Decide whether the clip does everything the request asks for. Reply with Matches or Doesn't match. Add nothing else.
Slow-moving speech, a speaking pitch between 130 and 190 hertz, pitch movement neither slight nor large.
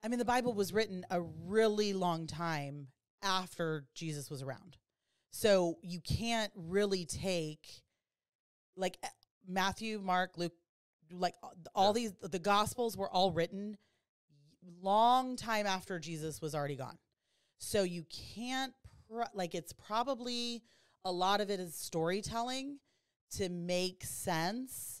Matches